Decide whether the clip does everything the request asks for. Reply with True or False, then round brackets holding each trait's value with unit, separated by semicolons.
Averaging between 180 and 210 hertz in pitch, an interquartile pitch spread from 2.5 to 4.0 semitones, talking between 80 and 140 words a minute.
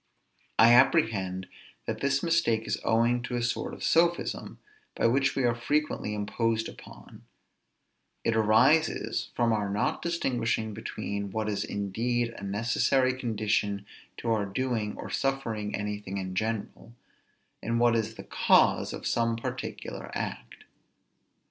False (115 Hz; 2.9 semitones; 135 wpm)